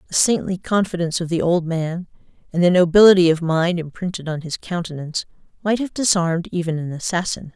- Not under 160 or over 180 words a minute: Yes, average, 175 wpm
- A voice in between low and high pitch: Yes, medium, 175 Hz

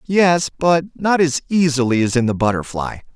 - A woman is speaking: No, male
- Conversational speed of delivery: Yes, average, 170 wpm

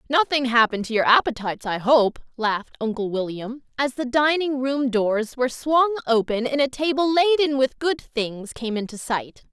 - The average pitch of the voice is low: No, very high, 255 Hz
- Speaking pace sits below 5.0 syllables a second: No, 5.2 syllables/s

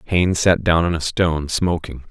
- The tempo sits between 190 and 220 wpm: Yes, average, 200 wpm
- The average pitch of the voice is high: No, very low, 85 Hz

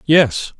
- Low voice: No, medium, 145 Hz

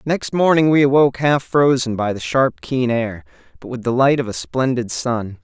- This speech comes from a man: Yes, male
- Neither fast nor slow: No, fast, 210 wpm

